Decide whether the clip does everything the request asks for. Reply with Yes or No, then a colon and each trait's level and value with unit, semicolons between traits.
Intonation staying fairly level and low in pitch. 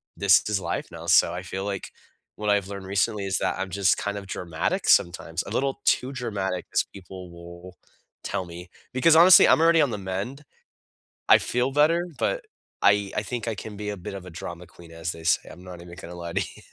No: average, 3.9 semitones; very low, 95 Hz